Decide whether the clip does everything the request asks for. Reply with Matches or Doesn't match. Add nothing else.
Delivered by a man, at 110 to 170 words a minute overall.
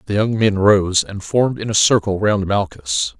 Doesn't match